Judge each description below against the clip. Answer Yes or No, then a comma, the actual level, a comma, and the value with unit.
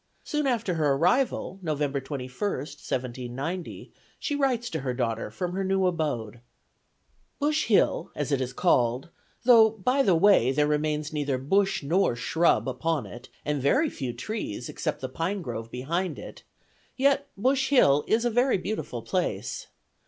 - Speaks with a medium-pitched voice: Yes, medium, 160 Hz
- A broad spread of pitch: Yes, wide, 8.4 semitones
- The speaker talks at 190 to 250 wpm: No, average, 155 wpm